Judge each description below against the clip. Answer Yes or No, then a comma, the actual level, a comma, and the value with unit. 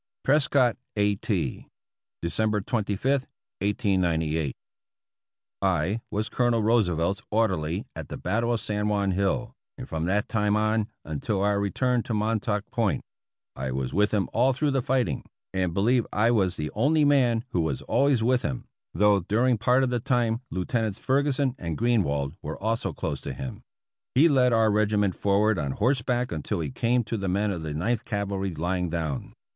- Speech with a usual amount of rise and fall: Yes, average, 4.8 semitones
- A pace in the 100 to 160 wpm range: No, average, 170 wpm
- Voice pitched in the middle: No, low, 105 Hz